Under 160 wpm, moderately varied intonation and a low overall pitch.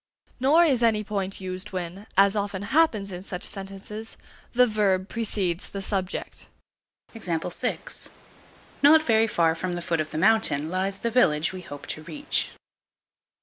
No: average, 150 wpm; average, 3.5 semitones; high, 195 Hz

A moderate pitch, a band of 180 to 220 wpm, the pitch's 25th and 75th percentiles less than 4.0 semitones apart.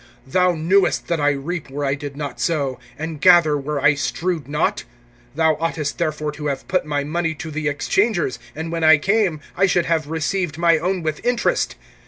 Yes: medium, 160 Hz; average, 195 wpm; average, 2.9 semitones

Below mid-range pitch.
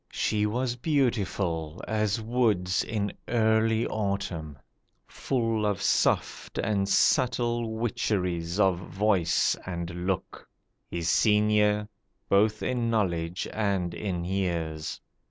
Yes: low, 105 Hz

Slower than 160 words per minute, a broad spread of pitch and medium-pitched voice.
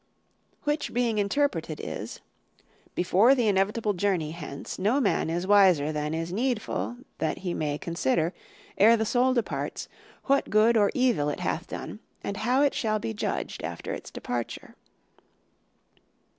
No: average, 145 wpm; wide, 6.3 semitones; high, 205 Hz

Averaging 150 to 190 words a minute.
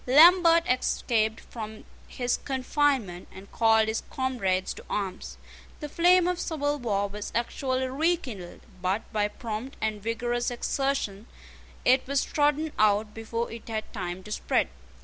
No: average, 140 wpm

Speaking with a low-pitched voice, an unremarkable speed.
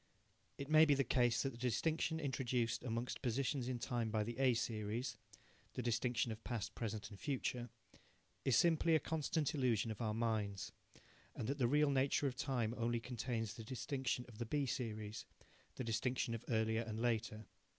Yes: low, 120 Hz; average, 180 wpm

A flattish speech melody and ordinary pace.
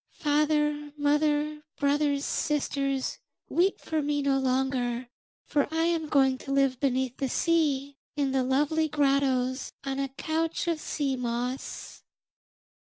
No: narrow, 2.1 semitones; slow, 130 wpm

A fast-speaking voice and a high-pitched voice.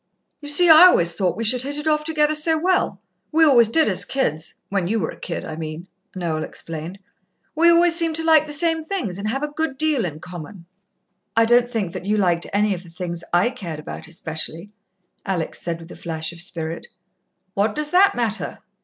Yes: fast, 215 wpm; high, 215 Hz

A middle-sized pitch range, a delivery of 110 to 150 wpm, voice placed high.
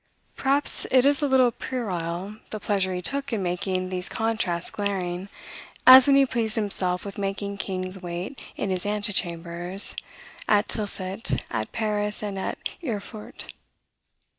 Yes: average, 3.4 semitones; average, 140 wpm; high, 200 Hz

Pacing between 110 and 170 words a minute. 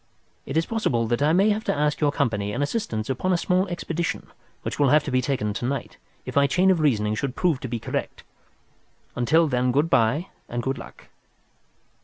No: fast, 205 wpm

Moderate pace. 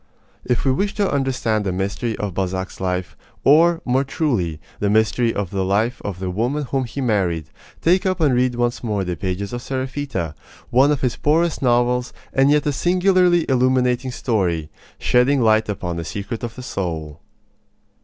Yes: average, 175 wpm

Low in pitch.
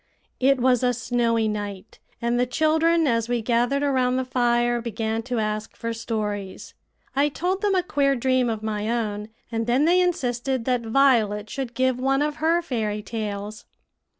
No: high, 240 Hz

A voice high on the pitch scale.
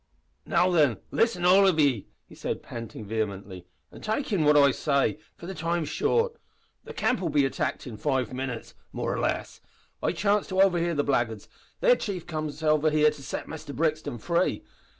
No: medium, 155 Hz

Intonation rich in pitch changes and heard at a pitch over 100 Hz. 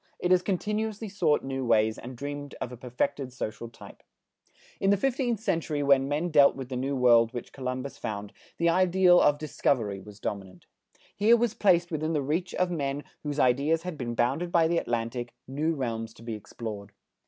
Yes: wide, 6.2 semitones; medium, 140 Hz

